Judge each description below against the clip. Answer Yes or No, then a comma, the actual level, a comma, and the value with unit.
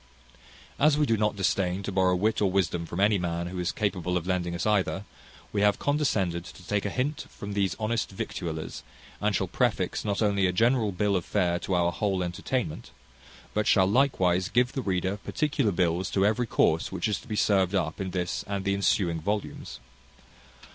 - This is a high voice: No, very low, 95 Hz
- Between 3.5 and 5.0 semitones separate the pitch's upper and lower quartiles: No, average, 2.8 semitones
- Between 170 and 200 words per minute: Yes, average, 195 wpm